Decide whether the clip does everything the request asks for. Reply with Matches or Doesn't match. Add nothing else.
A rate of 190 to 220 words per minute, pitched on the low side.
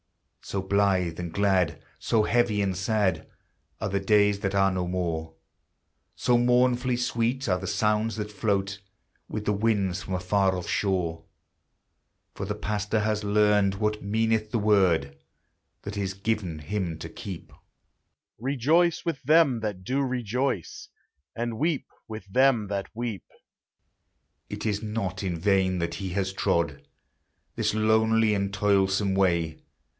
Doesn't match